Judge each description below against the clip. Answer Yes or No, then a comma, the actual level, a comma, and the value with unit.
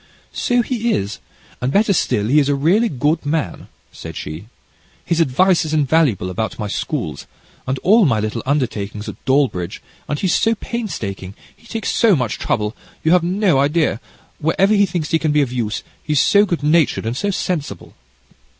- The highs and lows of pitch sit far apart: Yes, wide, 7.7 semitones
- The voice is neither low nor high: Yes, medium, 150 Hz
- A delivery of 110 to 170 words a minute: No, average, 180 wpm